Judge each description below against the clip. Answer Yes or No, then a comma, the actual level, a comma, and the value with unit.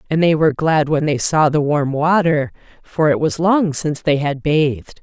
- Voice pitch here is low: No, medium, 155 Hz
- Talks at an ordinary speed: No, fast, 215 wpm